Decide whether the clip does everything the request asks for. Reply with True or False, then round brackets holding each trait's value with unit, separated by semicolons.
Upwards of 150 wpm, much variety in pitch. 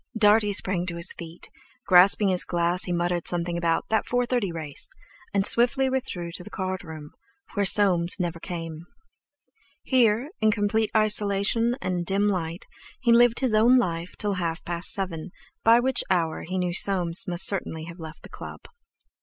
False (170 wpm; 3.9 semitones)